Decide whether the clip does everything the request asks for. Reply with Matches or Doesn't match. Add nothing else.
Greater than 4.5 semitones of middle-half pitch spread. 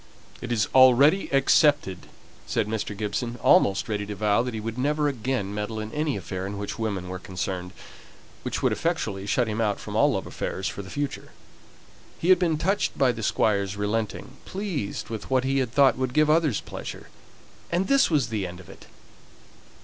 Matches